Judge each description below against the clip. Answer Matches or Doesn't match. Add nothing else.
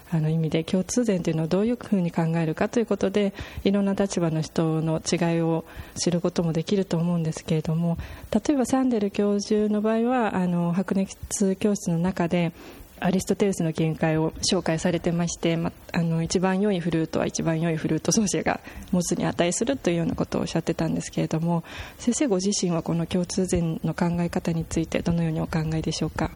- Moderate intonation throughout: Matches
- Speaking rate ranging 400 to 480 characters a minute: Matches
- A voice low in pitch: Doesn't match